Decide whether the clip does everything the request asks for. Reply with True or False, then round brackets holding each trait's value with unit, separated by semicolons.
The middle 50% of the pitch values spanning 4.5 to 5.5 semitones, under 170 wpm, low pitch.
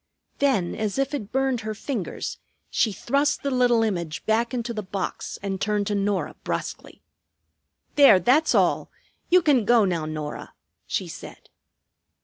False (5.2 semitones; 150 wpm; 220 Hz)